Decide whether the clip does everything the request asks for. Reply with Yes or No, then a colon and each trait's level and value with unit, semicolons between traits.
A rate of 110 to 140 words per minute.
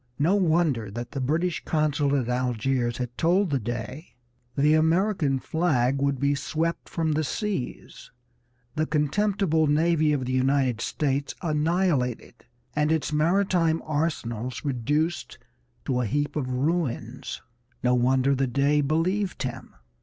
Yes: slow, 135 wpm